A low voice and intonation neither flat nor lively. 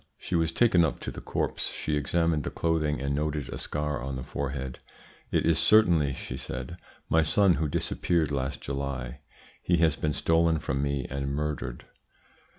Yes: very low, 75 Hz; average, 3.0 semitones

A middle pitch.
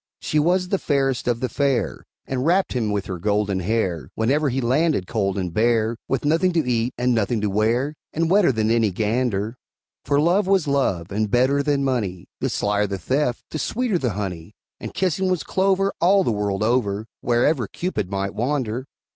No: low, 120 Hz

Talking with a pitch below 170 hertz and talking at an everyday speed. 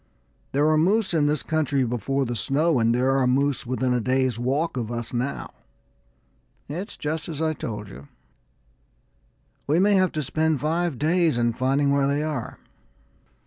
Yes: medium, 140 Hz; average, 170 wpm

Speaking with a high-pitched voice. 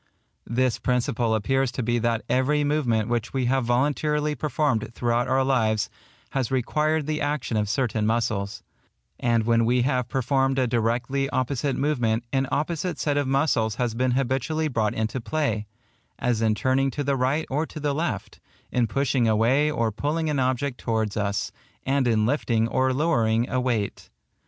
No: low, 125 Hz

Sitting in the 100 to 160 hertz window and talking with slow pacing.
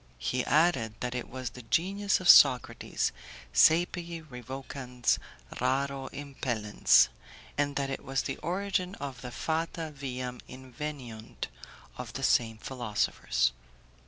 Yes: low, 135 Hz; slow, 125 wpm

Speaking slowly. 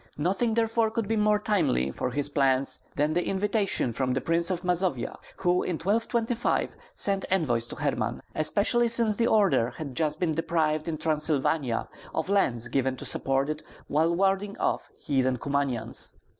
No: average, 165 wpm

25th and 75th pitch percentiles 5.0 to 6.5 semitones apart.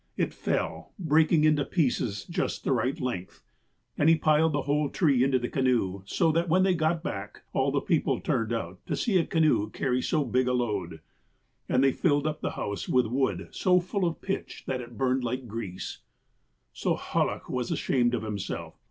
Yes: wide, 5.5 semitones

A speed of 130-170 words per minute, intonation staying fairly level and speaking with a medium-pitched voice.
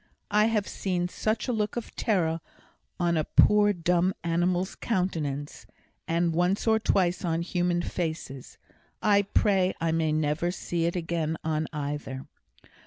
No: average, 145 wpm; average, 3.1 semitones; medium, 175 Hz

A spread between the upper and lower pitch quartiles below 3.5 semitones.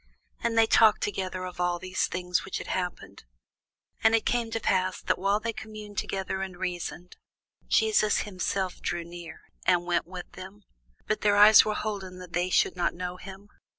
Yes: average, 2.8 semitones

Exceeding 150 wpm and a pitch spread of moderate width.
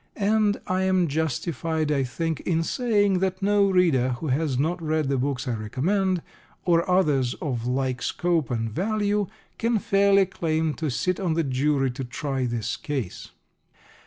No: average, 160 wpm; wide, 5.9 semitones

